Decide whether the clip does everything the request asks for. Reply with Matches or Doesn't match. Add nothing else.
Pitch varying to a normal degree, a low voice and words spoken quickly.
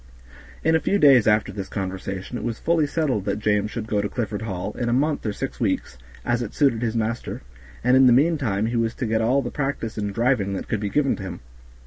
Matches